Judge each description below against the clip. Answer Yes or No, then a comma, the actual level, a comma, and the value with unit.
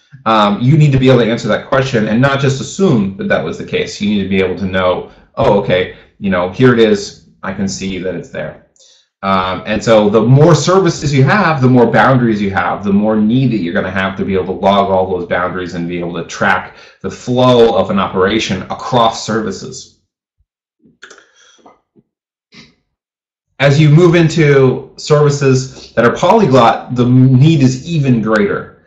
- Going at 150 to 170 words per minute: No, average, 195 wpm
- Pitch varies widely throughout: Yes, wide, 6.0 semitones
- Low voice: Yes, low, 120 Hz